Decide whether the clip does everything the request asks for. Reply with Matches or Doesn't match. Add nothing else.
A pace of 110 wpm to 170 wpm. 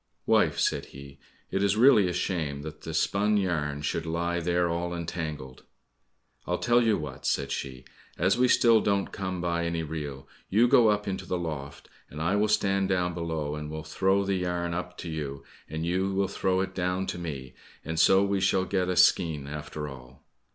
Doesn't match